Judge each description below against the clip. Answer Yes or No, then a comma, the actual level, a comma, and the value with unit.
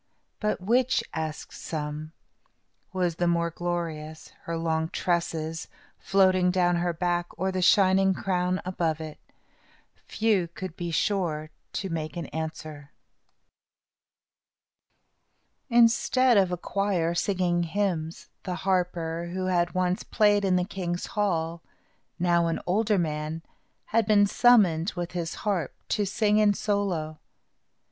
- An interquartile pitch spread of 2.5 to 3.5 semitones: Yes, average, 2.9 semitones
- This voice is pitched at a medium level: Yes, medium, 175 Hz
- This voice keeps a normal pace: No, slow, 125 wpm